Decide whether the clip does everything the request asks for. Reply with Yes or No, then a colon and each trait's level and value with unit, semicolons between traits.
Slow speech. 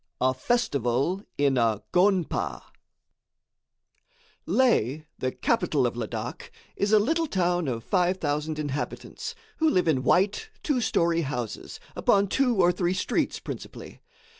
Yes: slow, 125 wpm